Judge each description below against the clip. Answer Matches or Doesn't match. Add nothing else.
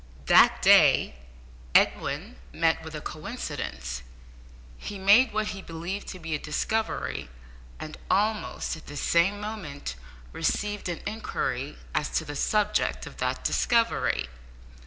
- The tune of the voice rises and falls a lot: Matches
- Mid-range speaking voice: Matches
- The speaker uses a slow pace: Matches